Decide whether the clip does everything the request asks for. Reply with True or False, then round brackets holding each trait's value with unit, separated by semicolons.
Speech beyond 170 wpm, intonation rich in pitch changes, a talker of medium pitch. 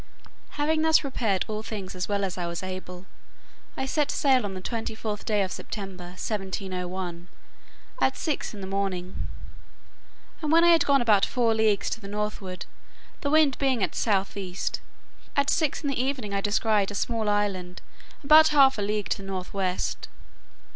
False (180 wpm; 5.8 semitones; 210 Hz)